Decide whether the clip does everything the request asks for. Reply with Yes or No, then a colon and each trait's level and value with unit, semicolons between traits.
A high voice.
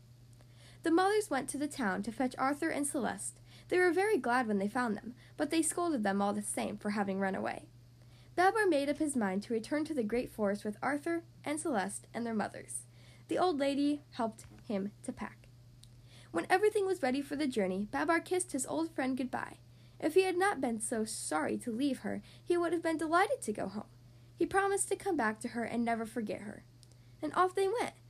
Yes: high, 245 Hz